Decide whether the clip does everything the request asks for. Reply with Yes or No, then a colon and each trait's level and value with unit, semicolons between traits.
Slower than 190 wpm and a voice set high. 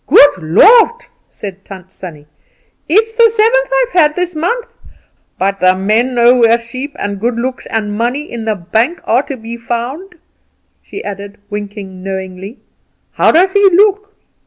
Yes: average, 160 wpm; high, 235 Hz